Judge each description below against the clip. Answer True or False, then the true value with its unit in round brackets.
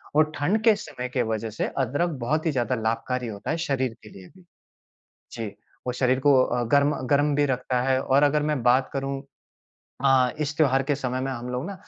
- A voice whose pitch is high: False (135 Hz)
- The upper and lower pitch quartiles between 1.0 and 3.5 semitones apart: True (2.7 semitones)